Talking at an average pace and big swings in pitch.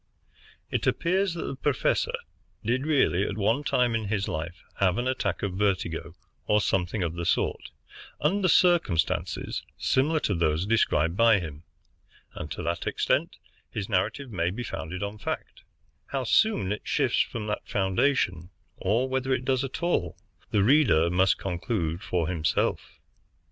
Yes: average, 155 wpm; wide, 6.8 semitones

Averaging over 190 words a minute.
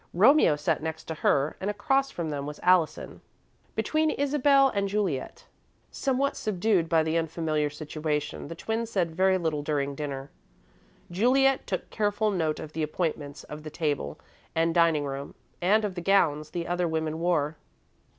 No: average, 160 wpm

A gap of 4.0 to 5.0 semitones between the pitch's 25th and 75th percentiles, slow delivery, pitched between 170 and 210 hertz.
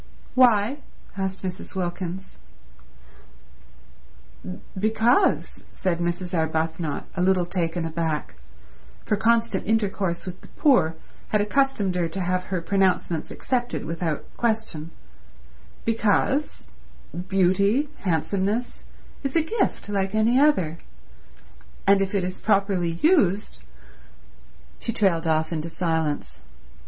Yes: average, 4.3 semitones; slow, 105 wpm; high, 190 Hz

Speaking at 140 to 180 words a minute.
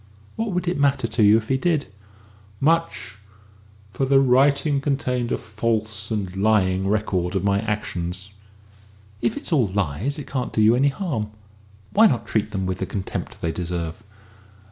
Yes: average, 170 wpm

